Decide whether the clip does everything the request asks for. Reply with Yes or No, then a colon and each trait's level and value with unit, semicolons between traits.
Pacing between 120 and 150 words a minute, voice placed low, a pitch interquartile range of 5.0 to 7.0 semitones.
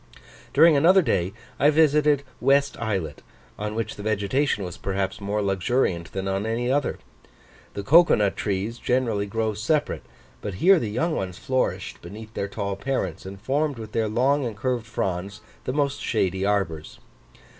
No: average, 165 wpm; low, 110 Hz; wide, 5.6 semitones